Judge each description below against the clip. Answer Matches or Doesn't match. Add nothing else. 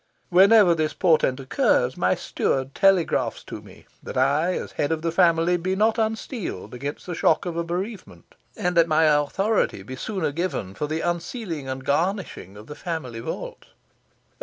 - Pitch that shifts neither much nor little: Matches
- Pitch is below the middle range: Doesn't match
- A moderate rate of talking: Matches